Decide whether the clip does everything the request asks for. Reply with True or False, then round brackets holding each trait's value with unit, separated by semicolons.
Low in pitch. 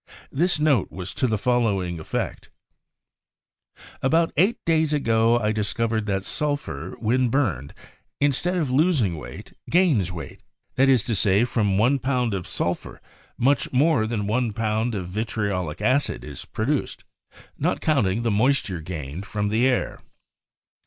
True (115 Hz)